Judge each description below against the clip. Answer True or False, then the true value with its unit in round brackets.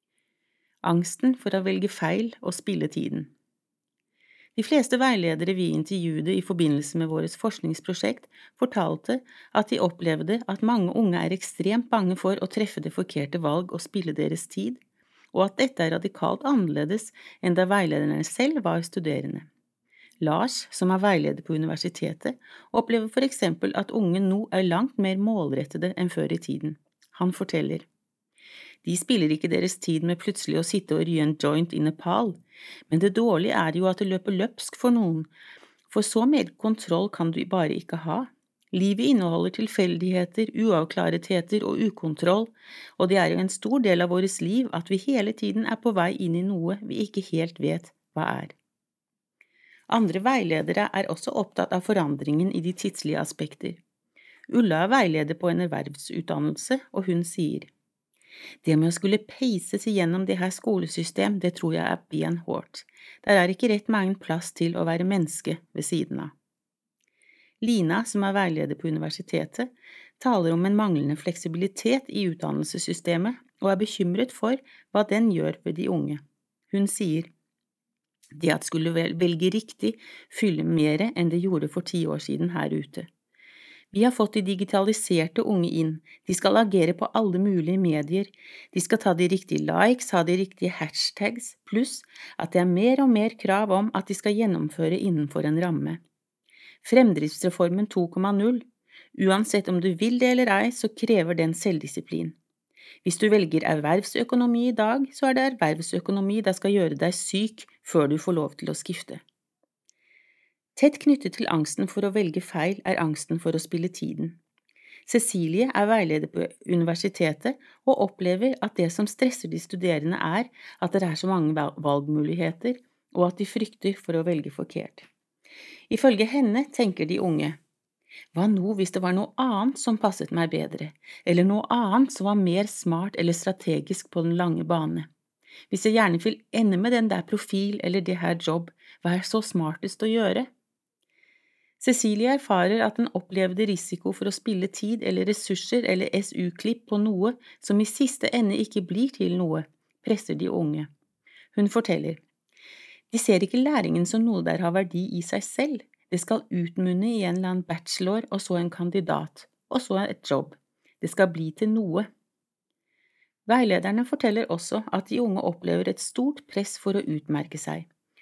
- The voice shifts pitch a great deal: False (4.8 semitones)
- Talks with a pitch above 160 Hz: True (190 Hz)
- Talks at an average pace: True (170 wpm)